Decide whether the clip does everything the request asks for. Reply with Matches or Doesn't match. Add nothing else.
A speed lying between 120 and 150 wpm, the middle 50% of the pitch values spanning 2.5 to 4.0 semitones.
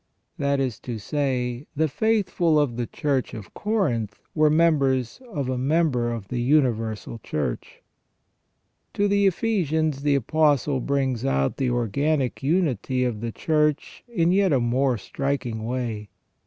Doesn't match